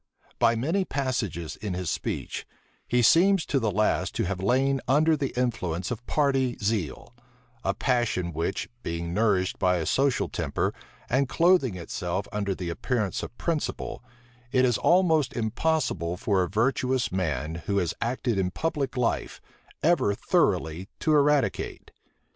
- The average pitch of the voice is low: Yes, low, 115 Hz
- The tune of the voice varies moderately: No, wide, 6.9 semitones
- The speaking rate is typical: Yes, average, 150 wpm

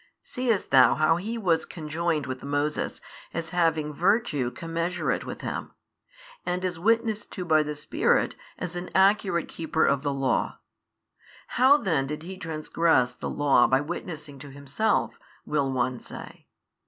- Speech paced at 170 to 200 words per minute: No, average, 150 wpm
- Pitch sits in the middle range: Yes, medium, 160 Hz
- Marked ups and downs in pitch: No, average, 4.0 semitones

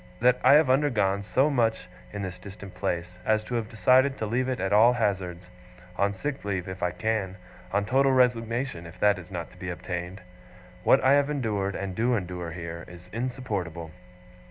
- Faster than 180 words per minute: Yes, average, 190 wpm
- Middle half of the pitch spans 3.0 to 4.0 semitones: No, wide, 5.6 semitones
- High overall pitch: No, low, 105 Hz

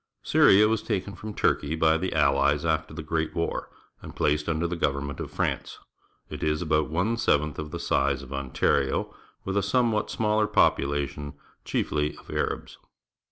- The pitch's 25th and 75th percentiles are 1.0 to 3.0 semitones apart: No, average, 4.5 semitones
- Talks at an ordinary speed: Yes, average, 170 wpm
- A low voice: Yes, very low, 80 Hz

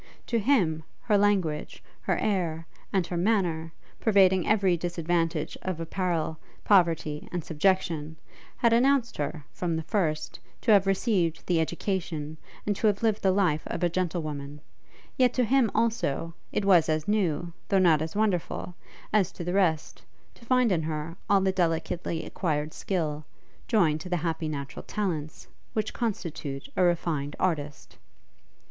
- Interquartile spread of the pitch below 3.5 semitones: No, average, 4.0 semitones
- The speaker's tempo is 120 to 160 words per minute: Yes, average, 155 wpm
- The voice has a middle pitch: Yes, medium, 175 Hz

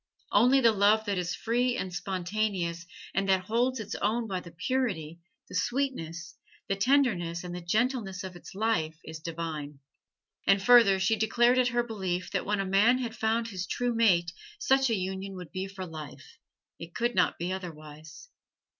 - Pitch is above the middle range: Yes, high, 195 Hz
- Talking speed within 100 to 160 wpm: No, average, 180 wpm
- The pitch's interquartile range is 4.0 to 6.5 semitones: Yes, average, 4.8 semitones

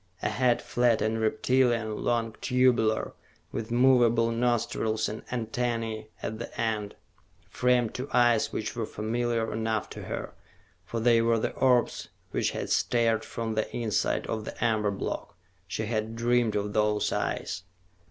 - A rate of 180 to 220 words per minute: No, average, 150 wpm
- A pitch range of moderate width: No, narrow, 1.7 semitones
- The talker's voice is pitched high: No, low, 115 Hz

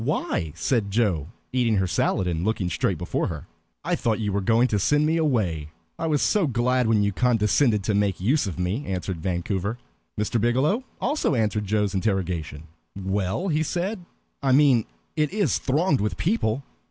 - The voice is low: Yes, low, 110 Hz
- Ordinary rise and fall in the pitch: No, wide, 6.2 semitones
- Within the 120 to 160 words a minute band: No, average, 175 wpm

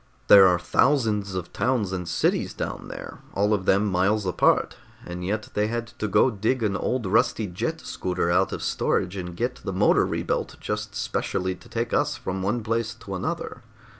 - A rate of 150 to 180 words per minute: No, average, 190 wpm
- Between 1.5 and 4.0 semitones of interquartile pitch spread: Yes, average, 3.2 semitones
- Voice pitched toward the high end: No, low, 100 Hz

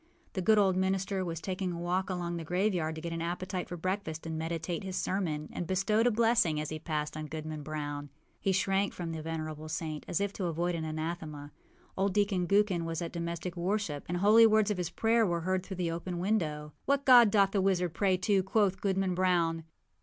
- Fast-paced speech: Yes, fast, 220 wpm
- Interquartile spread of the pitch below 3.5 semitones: Yes, average, 3.1 semitones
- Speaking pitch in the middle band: Yes, medium, 180 Hz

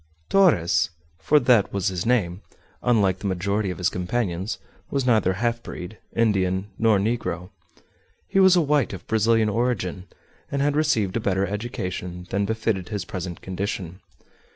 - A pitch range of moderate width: Yes, average, 4.1 semitones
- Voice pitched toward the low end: Yes, low, 100 Hz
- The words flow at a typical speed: Yes, average, 155 wpm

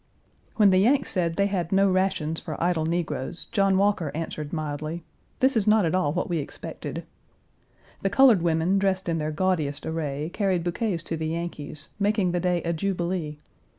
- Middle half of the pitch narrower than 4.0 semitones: Yes, average, 3.5 semitones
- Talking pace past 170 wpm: Yes, average, 180 wpm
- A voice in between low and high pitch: Yes, medium, 175 Hz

